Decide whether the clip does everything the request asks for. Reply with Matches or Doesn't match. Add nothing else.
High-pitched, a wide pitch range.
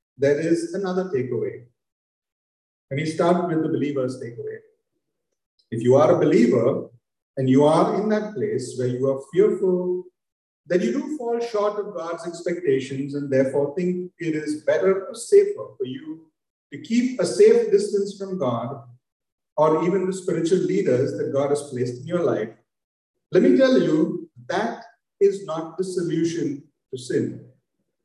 Doesn't match